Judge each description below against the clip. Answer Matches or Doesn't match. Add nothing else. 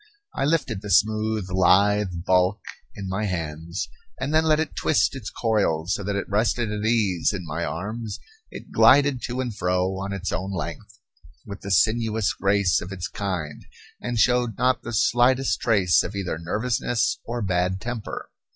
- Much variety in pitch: Doesn't match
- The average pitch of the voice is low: Matches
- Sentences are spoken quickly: Doesn't match